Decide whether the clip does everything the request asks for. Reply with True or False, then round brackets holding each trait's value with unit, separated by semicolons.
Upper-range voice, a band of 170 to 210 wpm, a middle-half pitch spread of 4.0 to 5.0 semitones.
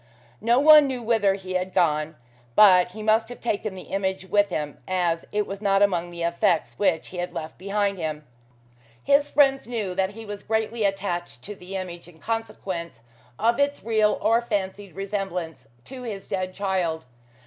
False (195 Hz; 180 wpm; 3.6 semitones)